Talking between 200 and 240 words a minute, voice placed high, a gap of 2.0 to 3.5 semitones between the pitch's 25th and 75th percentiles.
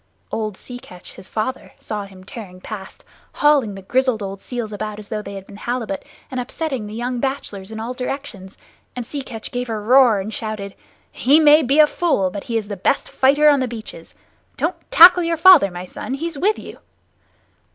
No: fast, 205 wpm; high, 230 Hz; average, 5.1 semitones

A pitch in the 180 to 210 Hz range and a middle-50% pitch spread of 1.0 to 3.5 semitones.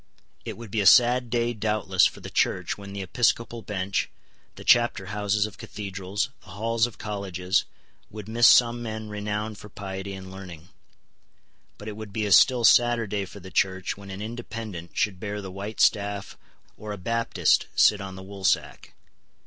No: low, 105 Hz; narrow, 2.5 semitones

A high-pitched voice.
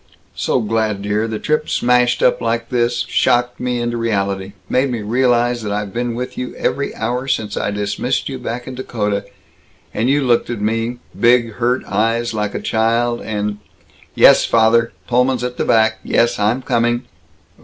No: low, 120 Hz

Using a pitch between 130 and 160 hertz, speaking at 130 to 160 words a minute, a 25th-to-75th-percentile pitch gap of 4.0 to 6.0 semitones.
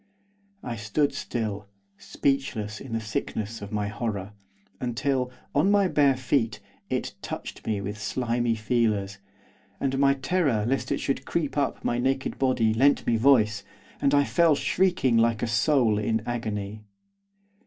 No: low, 120 Hz; average, 150 wpm; average, 4.3 semitones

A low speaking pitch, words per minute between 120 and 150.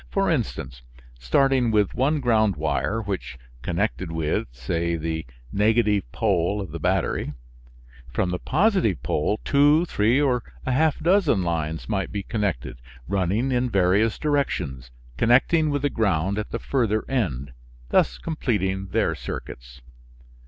Yes: low, 105 Hz; average, 140 wpm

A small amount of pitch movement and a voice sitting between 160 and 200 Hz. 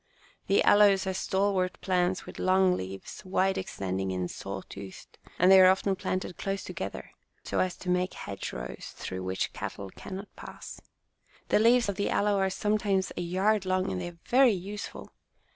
Yes: narrow, 1.9 semitones; medium, 185 Hz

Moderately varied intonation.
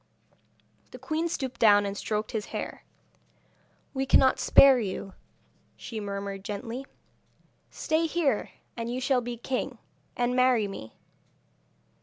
Yes: average, 4.4 semitones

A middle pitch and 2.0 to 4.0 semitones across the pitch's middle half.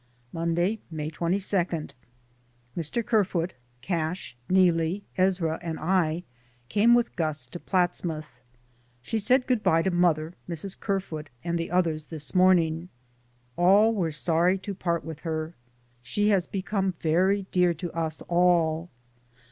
Yes: medium, 175 Hz; average, 2.9 semitones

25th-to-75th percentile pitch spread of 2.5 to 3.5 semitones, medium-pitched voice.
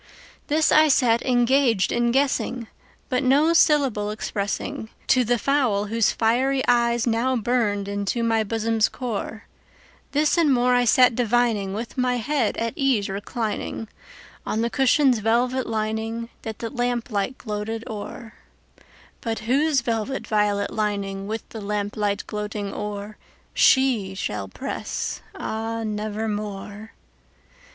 No: average, 3.1 semitones; high, 225 Hz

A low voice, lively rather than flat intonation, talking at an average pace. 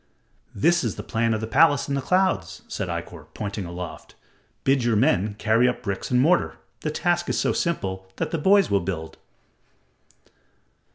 Yes: low, 115 Hz; wide, 8.3 semitones; average, 175 wpm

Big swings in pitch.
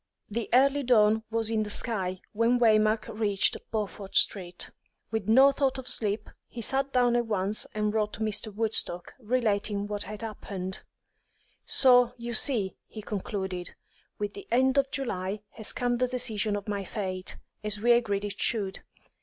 No: average, 2.9 semitones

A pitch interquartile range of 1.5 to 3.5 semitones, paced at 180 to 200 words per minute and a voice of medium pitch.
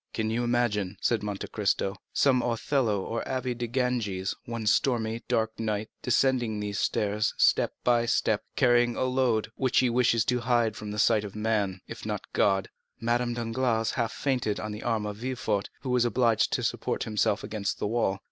No: narrow, 2.4 semitones; average, 185 wpm; low, 115 Hz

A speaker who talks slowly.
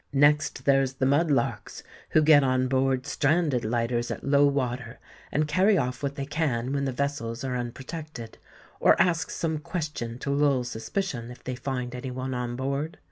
No: average, 180 wpm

